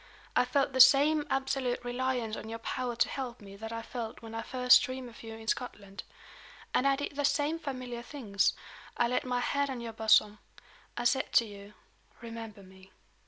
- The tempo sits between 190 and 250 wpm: Yes, average, 195 wpm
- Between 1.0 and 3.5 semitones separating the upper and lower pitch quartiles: Yes, average, 3.0 semitones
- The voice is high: Yes, high, 245 Hz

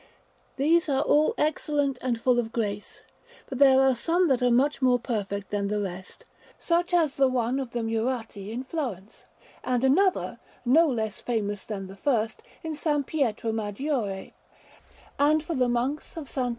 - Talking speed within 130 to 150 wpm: No, average, 170 wpm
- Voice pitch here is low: No, very high, 250 Hz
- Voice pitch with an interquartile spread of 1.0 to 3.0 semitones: No, average, 4.6 semitones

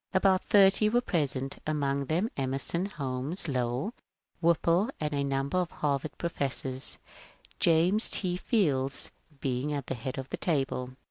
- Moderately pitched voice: Yes, medium, 145 Hz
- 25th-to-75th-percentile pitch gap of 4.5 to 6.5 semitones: Yes, average, 5.0 semitones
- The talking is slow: No, average, 145 wpm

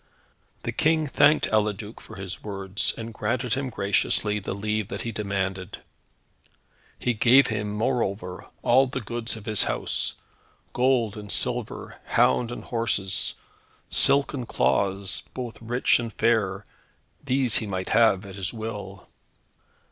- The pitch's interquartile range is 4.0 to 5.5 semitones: No, average, 3.5 semitones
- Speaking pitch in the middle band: No, low, 110 Hz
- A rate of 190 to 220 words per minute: No, slow, 135 wpm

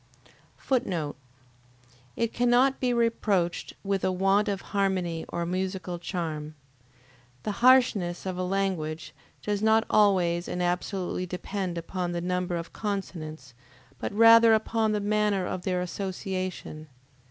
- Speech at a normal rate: No, slow, 130 wpm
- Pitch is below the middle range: No, high, 190 Hz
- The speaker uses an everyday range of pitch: Yes, average, 3.2 semitones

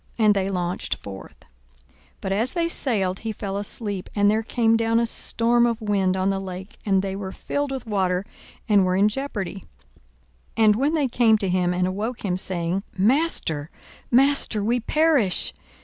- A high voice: Yes, high, 205 Hz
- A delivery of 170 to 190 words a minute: Yes, average, 180 wpm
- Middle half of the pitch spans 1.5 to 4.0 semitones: Yes, average, 3.7 semitones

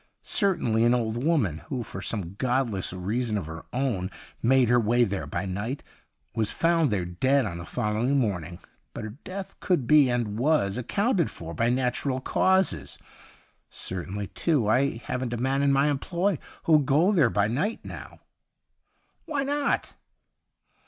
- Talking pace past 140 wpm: Yes, average, 160 wpm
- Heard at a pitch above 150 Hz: No, low, 125 Hz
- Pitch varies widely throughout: Yes, wide, 5.7 semitones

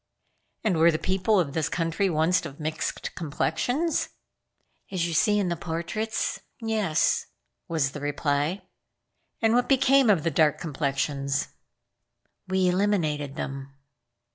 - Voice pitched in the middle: Yes, medium, 165 Hz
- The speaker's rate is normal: No, slow, 130 wpm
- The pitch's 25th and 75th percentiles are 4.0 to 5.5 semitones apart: Yes, average, 5.2 semitones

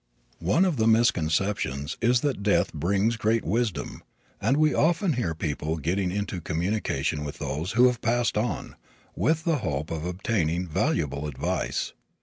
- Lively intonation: Yes, wide, 6.8 semitones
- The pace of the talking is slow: No, average, 155 wpm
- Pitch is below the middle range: Yes, low, 100 Hz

